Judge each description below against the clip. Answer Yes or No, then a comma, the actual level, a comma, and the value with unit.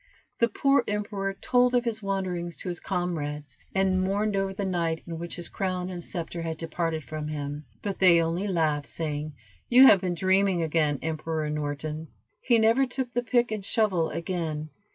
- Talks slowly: No, average, 180 wpm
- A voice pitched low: No, medium, 180 Hz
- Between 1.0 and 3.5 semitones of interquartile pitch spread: No, average, 3.9 semitones